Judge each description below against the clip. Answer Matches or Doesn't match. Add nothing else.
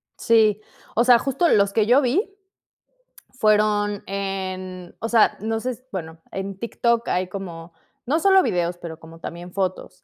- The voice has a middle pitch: Doesn't match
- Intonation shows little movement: Doesn't match